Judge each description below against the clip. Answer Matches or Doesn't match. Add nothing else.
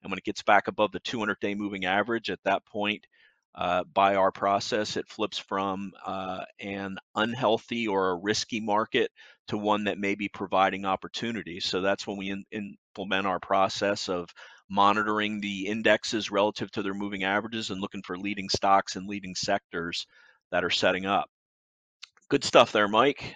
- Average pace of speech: Matches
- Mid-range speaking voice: Doesn't match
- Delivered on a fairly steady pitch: Matches